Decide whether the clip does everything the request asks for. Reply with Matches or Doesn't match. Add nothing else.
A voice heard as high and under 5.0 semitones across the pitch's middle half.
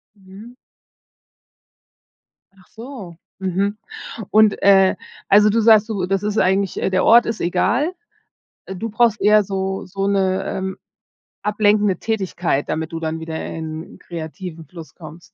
Matches